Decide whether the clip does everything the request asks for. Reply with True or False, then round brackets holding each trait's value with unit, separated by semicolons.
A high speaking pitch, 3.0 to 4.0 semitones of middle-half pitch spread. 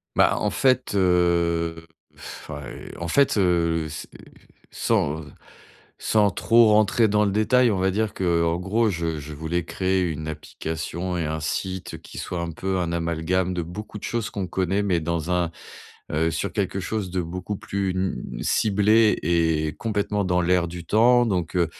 False (90 Hz; 3.5 semitones)